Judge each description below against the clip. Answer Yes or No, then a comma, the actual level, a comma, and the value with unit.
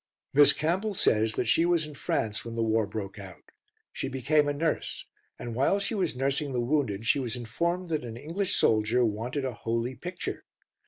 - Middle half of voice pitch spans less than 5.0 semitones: No, wide, 5.5 semitones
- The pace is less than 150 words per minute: No, average, 195 wpm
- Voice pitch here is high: No, low, 130 Hz